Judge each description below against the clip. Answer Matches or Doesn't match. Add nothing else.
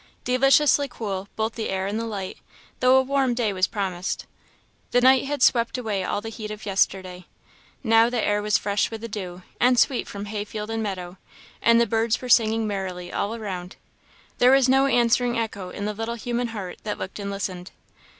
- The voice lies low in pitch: Doesn't match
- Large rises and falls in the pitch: Doesn't match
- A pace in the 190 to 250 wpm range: Matches